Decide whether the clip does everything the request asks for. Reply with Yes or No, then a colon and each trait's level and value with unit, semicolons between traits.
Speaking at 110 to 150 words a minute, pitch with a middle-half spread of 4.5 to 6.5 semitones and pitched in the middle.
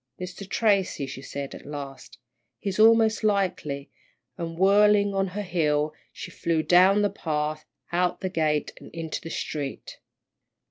Yes: average, 145 wpm; average, 4.8 semitones; medium, 180 Hz